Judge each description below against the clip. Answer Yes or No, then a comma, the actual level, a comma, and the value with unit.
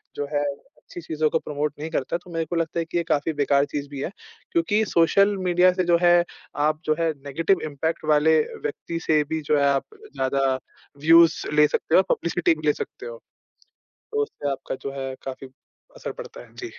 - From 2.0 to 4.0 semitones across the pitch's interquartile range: Yes, average, 2.8 semitones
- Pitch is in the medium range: Yes, medium, 160 Hz